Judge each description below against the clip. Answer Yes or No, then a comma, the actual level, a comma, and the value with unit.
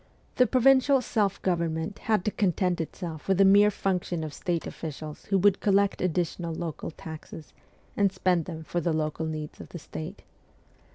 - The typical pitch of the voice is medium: Yes, medium, 175 Hz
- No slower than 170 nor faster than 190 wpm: Yes, average, 180 wpm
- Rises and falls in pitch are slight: No, average, 3.6 semitones